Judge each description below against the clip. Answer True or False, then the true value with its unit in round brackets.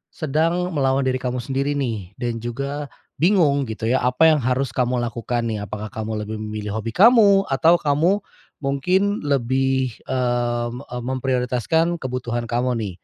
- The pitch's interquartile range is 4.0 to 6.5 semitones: False (3.5 semitones)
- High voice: False (130 Hz)